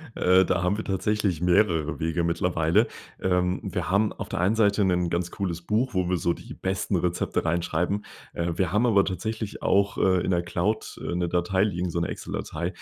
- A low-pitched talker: Yes, very low, 90 Hz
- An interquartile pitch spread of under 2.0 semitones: No, average, 2.7 semitones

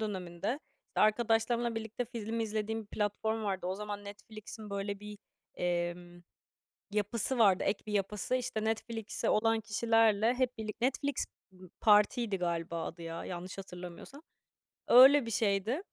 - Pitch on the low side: No, high, 215 Hz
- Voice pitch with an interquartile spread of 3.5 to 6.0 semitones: No, average, 2.8 semitones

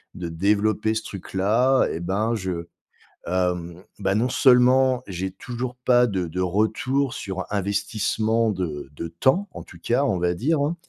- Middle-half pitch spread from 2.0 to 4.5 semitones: No, wide, 5.4 semitones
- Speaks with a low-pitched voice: Yes, low, 105 Hz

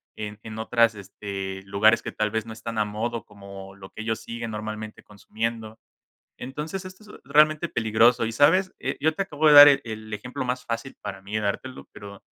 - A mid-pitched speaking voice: No, low, 110 Hz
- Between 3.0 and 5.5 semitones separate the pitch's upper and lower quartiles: Yes, average, 3.4 semitones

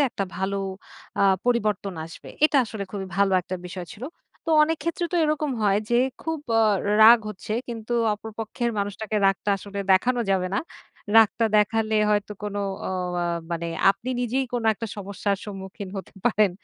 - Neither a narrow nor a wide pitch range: Yes, average, 3.2 semitones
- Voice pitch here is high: Yes, high, 210 Hz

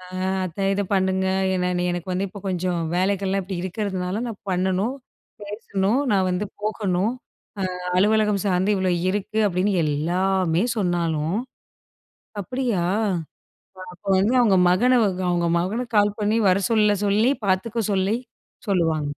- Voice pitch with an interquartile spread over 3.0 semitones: No, narrow, 2.4 semitones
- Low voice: No, high, 190 Hz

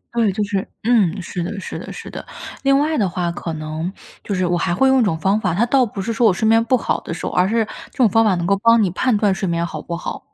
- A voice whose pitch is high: Yes, high, 200 Hz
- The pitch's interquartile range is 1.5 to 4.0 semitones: No, average, 4.5 semitones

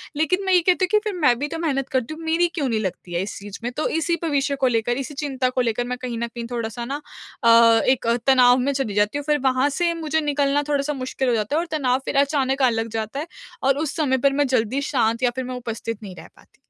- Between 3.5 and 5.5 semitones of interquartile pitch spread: Yes, average, 4.0 semitones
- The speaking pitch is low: No, very high, 265 Hz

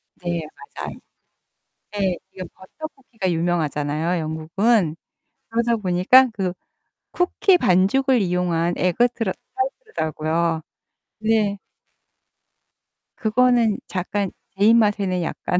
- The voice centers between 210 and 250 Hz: No, high, 190 Hz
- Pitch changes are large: No, average, 4.7 semitones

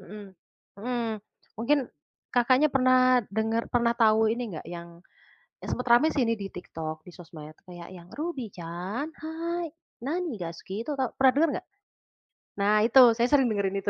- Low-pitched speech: No, high, 230 Hz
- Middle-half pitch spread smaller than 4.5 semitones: No, wide, 5.6 semitones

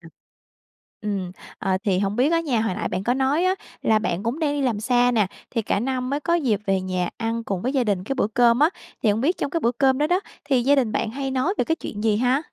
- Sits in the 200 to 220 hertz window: No, high, 245 Hz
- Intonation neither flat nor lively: Yes, average, 4.9 semitones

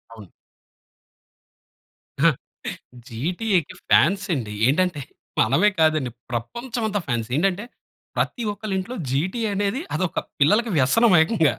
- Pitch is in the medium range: Yes, medium, 180 Hz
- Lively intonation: Yes, wide, 7.3 semitones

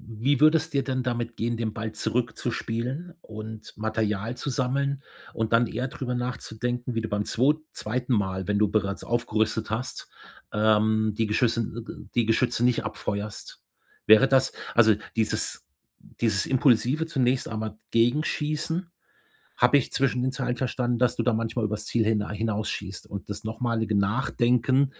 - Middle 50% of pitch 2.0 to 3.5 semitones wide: Yes, average, 2.7 semitones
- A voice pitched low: Yes, low, 115 Hz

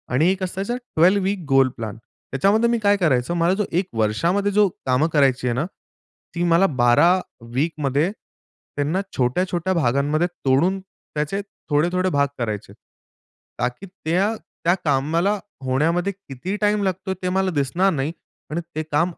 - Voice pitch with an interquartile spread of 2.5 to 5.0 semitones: No, wide, 5.6 semitones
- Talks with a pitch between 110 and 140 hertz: No, medium, 170 Hz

